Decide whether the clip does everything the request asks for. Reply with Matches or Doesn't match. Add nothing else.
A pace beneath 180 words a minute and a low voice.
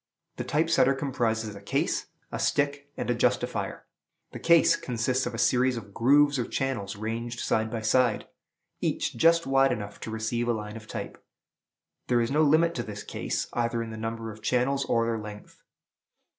Doesn't match